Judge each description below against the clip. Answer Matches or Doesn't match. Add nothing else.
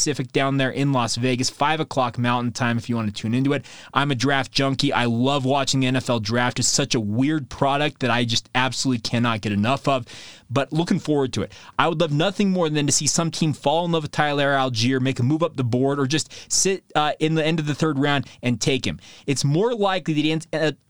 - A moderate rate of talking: Doesn't match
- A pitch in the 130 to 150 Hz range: Matches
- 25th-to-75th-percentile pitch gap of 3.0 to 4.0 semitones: Matches